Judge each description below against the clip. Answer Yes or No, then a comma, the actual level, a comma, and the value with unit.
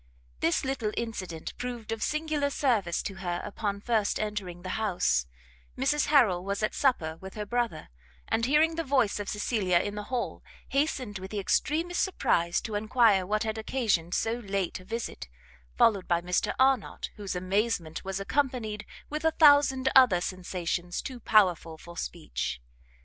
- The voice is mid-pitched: No, high, 210 Hz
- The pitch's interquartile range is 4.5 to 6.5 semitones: Yes, wide, 5.6 semitones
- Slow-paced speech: No, average, 160 wpm